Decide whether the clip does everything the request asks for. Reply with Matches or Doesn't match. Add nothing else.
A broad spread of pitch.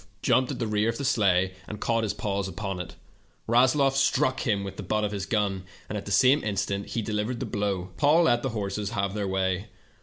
Doesn't match